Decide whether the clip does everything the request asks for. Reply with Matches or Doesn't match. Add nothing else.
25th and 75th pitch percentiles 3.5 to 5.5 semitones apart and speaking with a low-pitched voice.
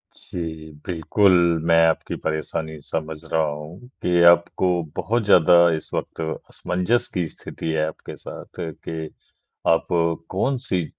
Doesn't match